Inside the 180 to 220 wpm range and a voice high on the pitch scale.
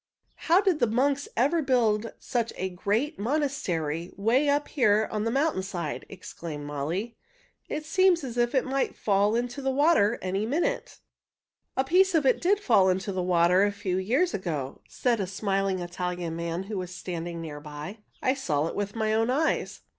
Yes: average, 185 wpm; high, 215 Hz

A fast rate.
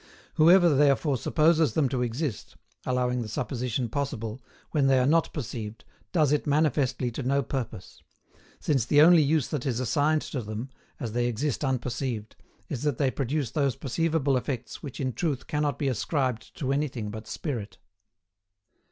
No: average, 160 wpm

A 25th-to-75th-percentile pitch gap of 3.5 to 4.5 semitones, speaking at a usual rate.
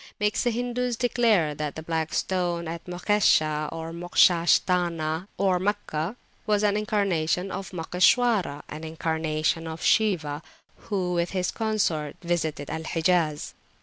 No: average, 4.2 semitones; slow, 130 wpm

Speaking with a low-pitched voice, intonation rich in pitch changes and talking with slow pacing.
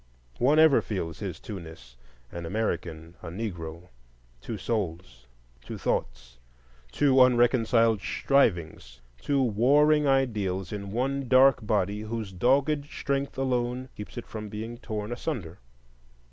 Yes: low, 110 Hz; wide, 7.0 semitones; slow, 120 wpm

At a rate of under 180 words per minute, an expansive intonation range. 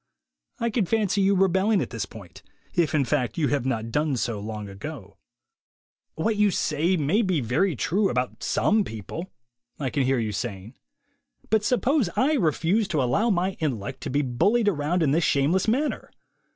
No: average, 185 wpm; wide, 8.0 semitones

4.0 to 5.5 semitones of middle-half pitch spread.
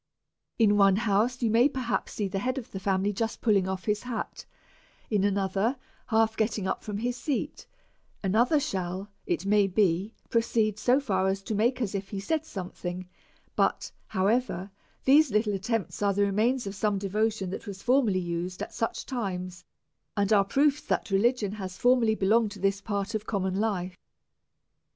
No: average, 3.2 semitones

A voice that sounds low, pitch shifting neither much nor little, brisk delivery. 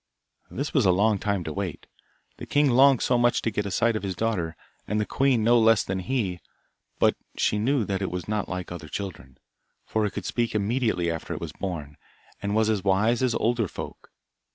Yes: low, 105 Hz; average, 4.1 semitones; fast, 215 wpm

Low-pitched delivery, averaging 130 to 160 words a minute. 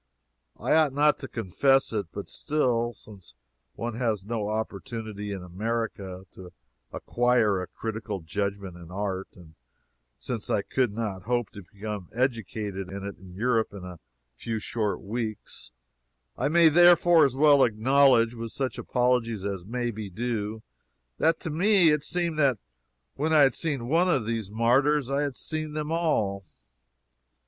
Yes: low, 115 Hz; average, 155 wpm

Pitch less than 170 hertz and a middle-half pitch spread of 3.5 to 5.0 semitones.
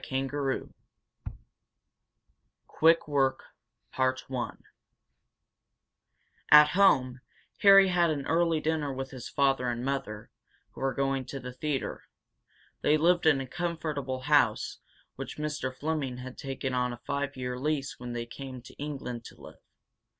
No: low, 135 Hz; average, 2.9 semitones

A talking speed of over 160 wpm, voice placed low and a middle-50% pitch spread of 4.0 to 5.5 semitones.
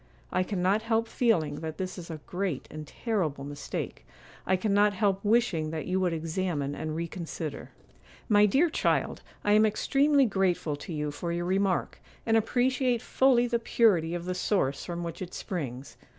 No: average, 170 wpm; medium, 185 Hz; average, 5.2 semitones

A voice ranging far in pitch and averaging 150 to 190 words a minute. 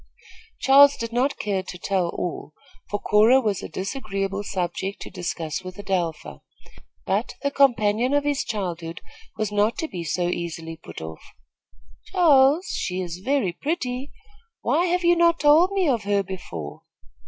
Yes: wide, 7.6 semitones; average, 155 wpm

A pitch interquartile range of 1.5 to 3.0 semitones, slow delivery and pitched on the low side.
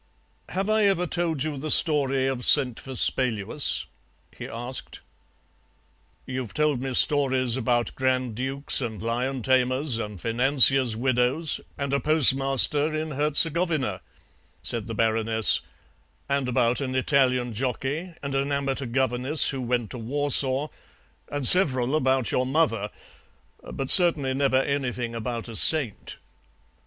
Yes: average, 2.7 semitones; slow, 130 wpm; low, 130 Hz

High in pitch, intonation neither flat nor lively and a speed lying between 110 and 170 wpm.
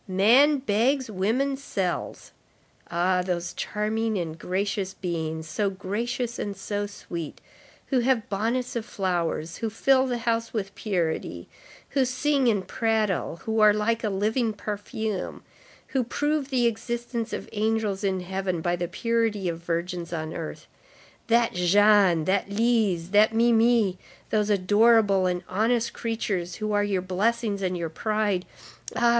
Yes: high, 210 Hz; average, 3.9 semitones; average, 145 wpm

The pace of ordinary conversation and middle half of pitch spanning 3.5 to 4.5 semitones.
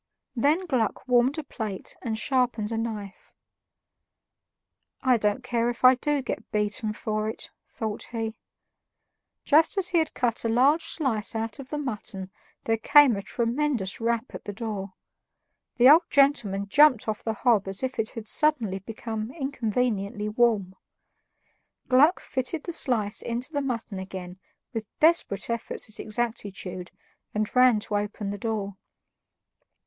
Yes: average, 150 wpm; average, 3.8 semitones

